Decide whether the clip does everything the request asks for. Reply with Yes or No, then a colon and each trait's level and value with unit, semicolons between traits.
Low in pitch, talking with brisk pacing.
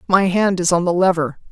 No: medium, 180 Hz; fast, 240 wpm